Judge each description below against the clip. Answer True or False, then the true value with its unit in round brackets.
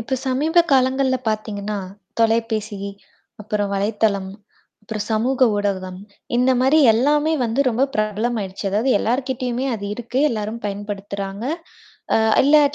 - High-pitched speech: True (220 Hz)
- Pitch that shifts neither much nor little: True (3.9 semitones)